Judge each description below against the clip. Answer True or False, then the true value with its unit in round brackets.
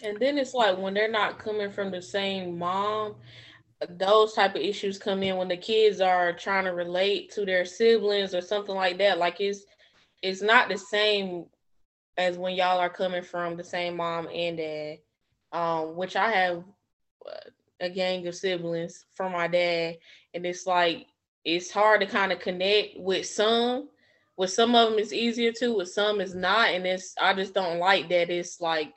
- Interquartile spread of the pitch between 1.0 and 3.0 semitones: True (2.7 semitones)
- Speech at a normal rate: True (190 wpm)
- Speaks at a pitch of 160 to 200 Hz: True (185 Hz)